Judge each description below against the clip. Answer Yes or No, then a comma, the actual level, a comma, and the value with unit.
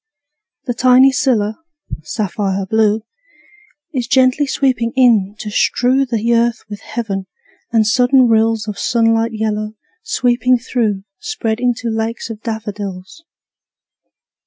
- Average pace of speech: No, slow, 115 wpm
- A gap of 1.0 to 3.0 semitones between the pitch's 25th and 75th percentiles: Yes, average, 2.7 semitones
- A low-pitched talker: No, high, 225 Hz